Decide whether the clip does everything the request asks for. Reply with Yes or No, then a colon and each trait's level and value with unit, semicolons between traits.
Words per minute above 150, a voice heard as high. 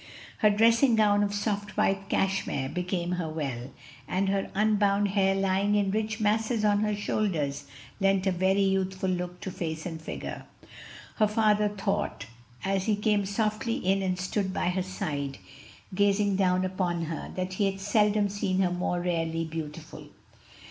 Yes: average, 160 wpm; high, 195 Hz